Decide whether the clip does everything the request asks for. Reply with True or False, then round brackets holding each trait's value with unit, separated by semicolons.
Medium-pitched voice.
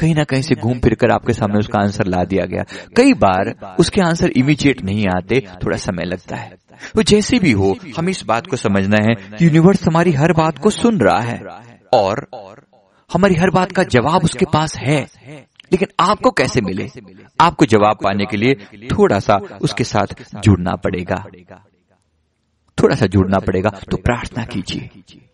False (125 Hz)